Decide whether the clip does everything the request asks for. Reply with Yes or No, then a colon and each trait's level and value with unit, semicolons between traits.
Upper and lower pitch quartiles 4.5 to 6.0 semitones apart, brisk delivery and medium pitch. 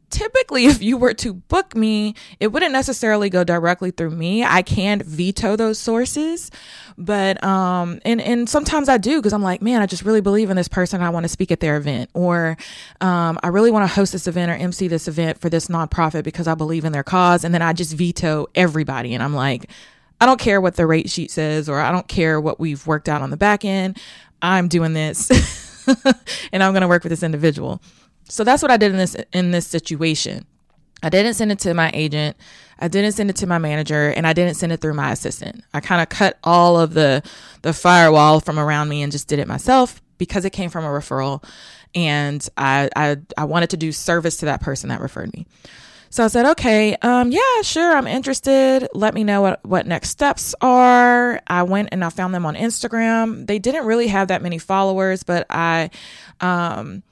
Yes: average, 4.9 semitones; fast, 220 wpm; medium, 180 Hz